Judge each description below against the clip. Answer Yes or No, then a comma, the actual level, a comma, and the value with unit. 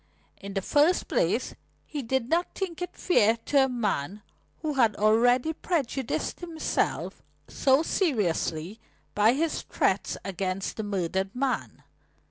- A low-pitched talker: No, high, 245 Hz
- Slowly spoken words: Yes, slow, 130 wpm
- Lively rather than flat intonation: Yes, wide, 7.0 semitones